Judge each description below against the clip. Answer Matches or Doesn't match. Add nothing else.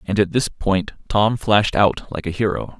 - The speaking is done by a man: Matches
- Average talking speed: Doesn't match